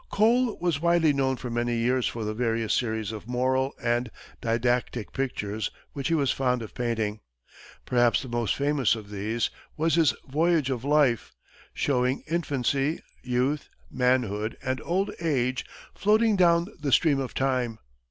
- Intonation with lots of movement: No, average, 4.0 semitones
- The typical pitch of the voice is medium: No, low, 130 Hz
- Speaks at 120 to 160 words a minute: Yes, average, 150 wpm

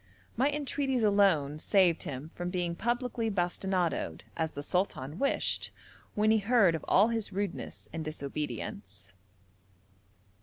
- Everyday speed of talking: No, slow, 125 wpm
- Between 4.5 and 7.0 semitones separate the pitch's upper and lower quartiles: Yes, wide, 5.6 semitones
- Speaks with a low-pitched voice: No, high, 190 Hz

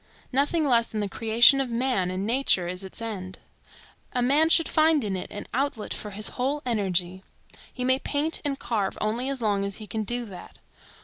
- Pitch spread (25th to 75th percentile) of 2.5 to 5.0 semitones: No, wide, 5.4 semitones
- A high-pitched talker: Yes, high, 230 Hz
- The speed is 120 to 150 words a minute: No, average, 200 wpm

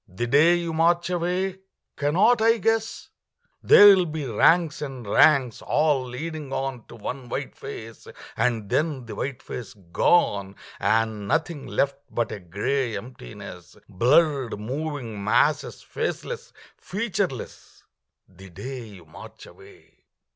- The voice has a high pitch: No, low, 135 Hz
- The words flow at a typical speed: No, slow, 130 wpm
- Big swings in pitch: Yes, wide, 6.7 semitones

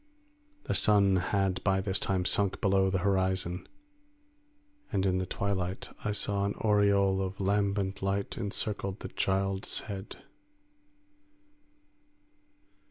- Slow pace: Yes, slow, 115 wpm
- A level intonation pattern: Yes, narrow, 1.0 semitones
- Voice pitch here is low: Yes, very low, 95 Hz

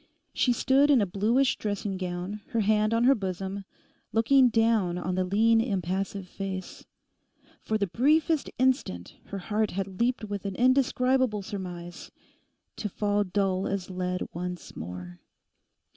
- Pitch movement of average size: Yes, average, 3.9 semitones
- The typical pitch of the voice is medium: No, high, 205 Hz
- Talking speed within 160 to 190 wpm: No, average, 145 wpm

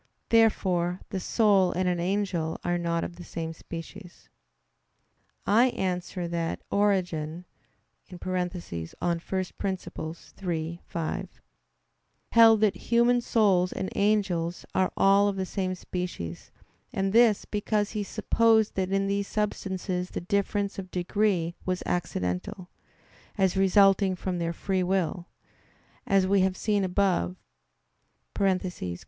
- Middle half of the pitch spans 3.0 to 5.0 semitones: No, narrow, 2.4 semitones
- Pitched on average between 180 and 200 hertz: Yes, medium, 185 Hz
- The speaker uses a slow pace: Yes, slow, 120 wpm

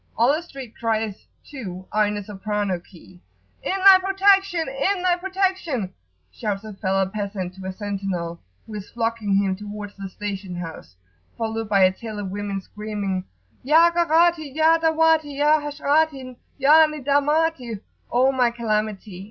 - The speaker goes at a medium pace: Yes, average, 150 wpm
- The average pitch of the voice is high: Yes, high, 225 Hz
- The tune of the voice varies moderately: No, wide, 7.6 semitones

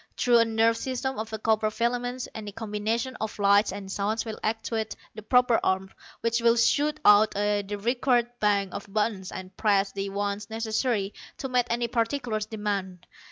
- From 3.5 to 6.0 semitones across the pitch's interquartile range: No, narrow, 2.5 semitones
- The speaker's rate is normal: Yes, average, 170 wpm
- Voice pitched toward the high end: Yes, high, 220 Hz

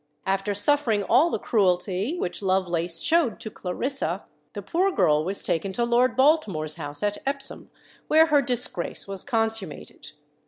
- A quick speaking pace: No, average, 150 wpm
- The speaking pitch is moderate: No, high, 210 Hz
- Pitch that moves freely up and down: Yes, wide, 7.0 semitones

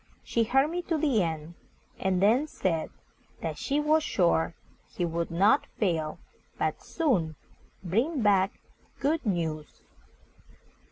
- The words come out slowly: Yes, slow, 125 wpm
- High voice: Yes, high, 195 Hz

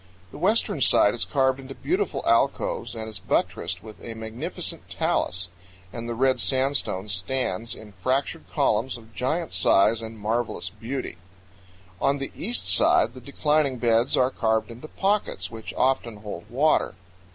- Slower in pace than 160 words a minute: Yes, average, 150 wpm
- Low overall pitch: Yes, low, 120 Hz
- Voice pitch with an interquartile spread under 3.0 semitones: No, average, 3.8 semitones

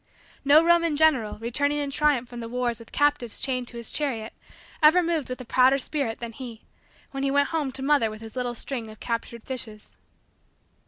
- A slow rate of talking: No, average, 200 wpm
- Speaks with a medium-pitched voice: No, very high, 255 Hz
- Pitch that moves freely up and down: No, average, 3.8 semitones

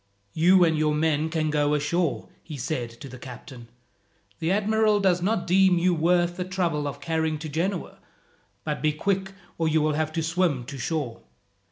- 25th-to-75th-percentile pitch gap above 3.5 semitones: No, average, 3.2 semitones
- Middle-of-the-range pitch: Yes, medium, 160 Hz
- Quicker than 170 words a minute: Yes, average, 185 wpm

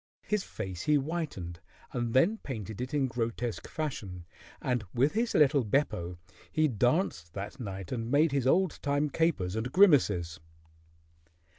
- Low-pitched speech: Yes, low, 125 Hz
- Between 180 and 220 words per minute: No, average, 145 wpm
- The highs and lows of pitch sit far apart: Yes, wide, 6.7 semitones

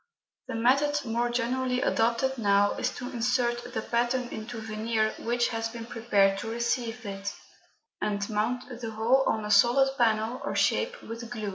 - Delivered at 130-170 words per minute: Yes, average, 165 wpm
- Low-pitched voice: No, high, 235 Hz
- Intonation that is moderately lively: No, narrow, 2.0 semitones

